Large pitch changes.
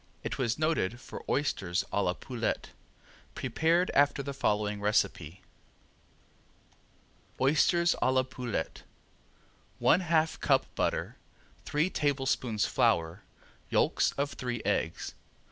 Yes: wide, 6.0 semitones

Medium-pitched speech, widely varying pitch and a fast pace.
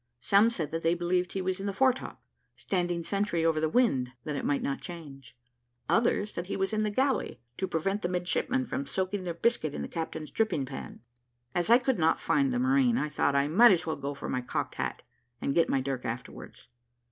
Yes: medium, 180 Hz; wide, 5.7 semitones; fast, 220 wpm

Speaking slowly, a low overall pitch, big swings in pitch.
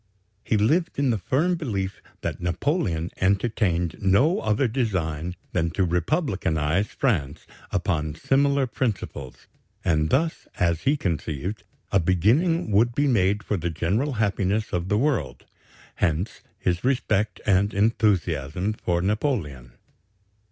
Yes: slow, 125 wpm; low, 100 Hz; wide, 6.1 semitones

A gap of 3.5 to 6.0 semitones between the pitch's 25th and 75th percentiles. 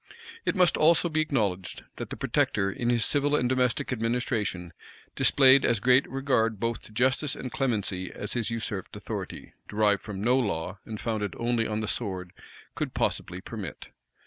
Yes: average, 4.0 semitones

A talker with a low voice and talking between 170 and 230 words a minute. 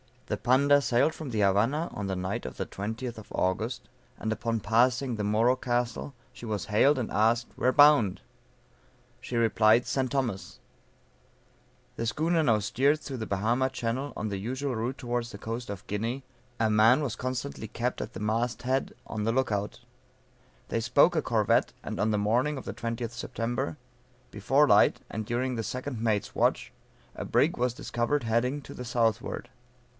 Yes: low, 120 Hz; average, 175 wpm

